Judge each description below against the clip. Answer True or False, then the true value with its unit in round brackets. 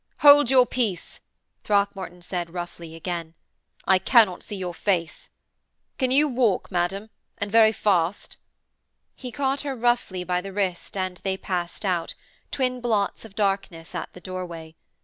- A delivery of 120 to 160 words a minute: True (150 wpm)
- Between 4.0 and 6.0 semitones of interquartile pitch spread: True (4.5 semitones)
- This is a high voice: True (195 Hz)